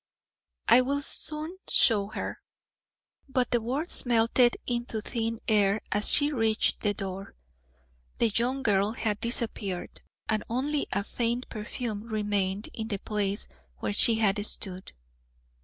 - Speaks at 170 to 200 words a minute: No, average, 140 wpm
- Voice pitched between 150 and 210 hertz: No, high, 225 Hz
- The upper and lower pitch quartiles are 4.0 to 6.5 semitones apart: No, average, 3.1 semitones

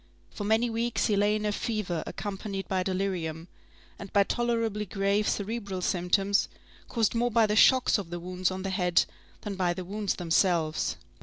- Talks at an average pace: Yes, average, 175 wpm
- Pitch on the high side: Yes, high, 200 Hz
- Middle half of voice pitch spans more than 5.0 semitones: No, average, 2.7 semitones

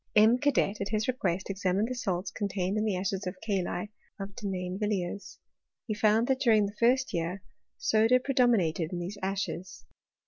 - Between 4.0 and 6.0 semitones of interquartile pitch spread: No, average, 3.3 semitones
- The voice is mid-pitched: No, high, 205 Hz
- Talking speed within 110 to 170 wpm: No, average, 180 wpm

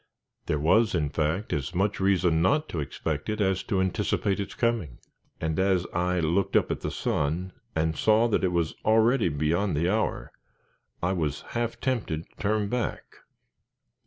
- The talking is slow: No, average, 170 wpm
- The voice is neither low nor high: No, very low, 95 Hz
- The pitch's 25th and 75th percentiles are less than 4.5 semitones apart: No, average, 4.9 semitones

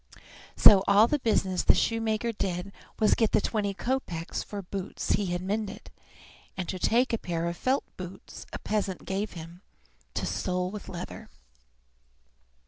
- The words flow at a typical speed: Yes, average, 160 wpm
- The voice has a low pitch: No, high, 200 Hz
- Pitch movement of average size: Yes, average, 3.2 semitones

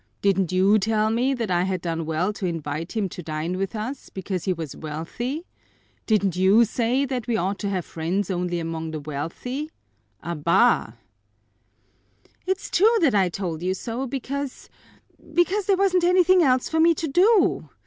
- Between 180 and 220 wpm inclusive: No, average, 170 wpm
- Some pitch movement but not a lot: No, wide, 7.7 semitones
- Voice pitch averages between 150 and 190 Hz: No, high, 200 Hz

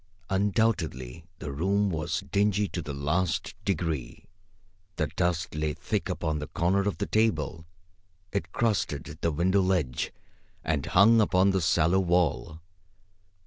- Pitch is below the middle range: Yes, very low, 90 Hz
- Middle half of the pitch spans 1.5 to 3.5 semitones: No, average, 4.0 semitones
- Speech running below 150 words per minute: Yes, slow, 135 wpm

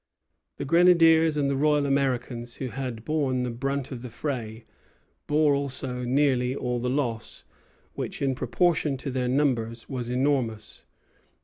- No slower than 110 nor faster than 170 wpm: Yes, average, 145 wpm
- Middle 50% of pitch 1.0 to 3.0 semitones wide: Yes, average, 2.7 semitones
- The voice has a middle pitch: No, low, 130 Hz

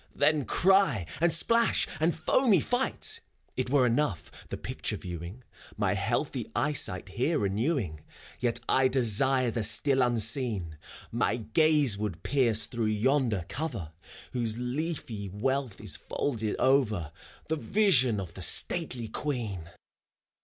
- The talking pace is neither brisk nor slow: No, slow, 130 wpm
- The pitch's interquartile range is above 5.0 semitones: Yes, wide, 5.6 semitones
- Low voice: Yes, low, 125 Hz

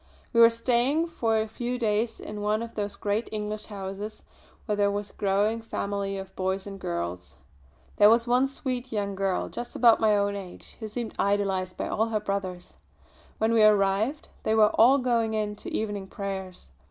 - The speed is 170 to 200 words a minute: Yes, average, 190 wpm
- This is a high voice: Yes, high, 210 Hz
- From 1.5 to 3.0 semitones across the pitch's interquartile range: Yes, narrow, 2.6 semitones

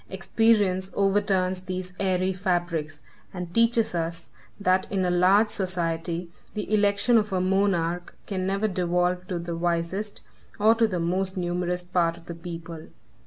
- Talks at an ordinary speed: Yes, average, 150 wpm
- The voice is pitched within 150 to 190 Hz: Yes, medium, 185 Hz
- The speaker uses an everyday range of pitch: No, narrow, 2.3 semitones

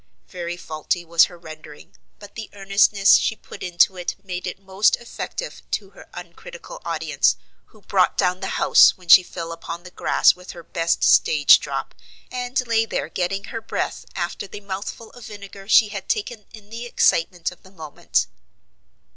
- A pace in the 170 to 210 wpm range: Yes, average, 175 wpm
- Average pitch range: Yes, average, 3.5 semitones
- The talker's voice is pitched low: No, high, 190 Hz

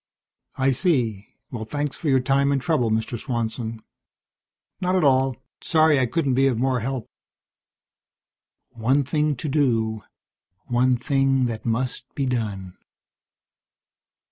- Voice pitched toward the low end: Yes, low, 130 Hz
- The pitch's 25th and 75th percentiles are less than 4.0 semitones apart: Yes, average, 3.4 semitones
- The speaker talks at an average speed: No, slow, 130 wpm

